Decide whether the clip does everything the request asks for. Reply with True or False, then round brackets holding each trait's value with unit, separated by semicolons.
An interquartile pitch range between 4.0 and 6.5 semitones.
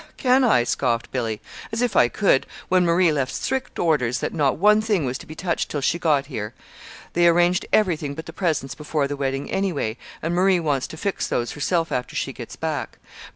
True (5.2 semitones)